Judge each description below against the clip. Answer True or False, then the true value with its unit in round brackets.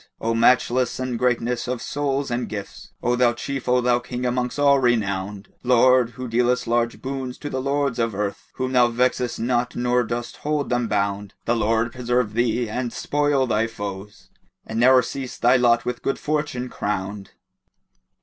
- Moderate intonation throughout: False (1.8 semitones)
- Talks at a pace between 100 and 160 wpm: False (185 wpm)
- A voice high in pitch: False (120 Hz)